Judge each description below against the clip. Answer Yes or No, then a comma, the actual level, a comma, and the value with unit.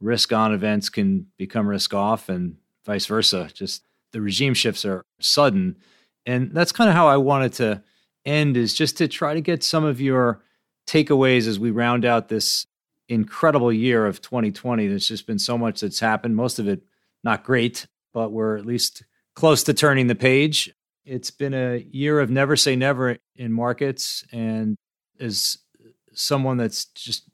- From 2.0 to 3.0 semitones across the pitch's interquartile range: No, average, 4.4 semitones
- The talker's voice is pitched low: Yes, low, 120 Hz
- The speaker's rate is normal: Yes, average, 175 wpm